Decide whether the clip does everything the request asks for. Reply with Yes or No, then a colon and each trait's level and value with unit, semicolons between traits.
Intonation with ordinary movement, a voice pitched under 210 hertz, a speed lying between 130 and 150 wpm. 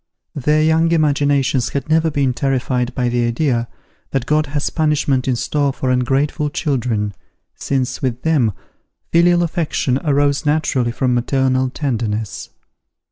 Yes: average, 3.2 semitones; low, 135 Hz; slow, 135 wpm